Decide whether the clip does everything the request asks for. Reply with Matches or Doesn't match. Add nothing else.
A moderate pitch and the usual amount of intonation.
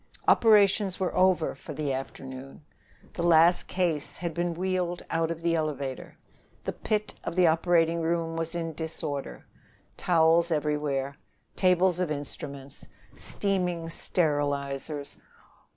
Matches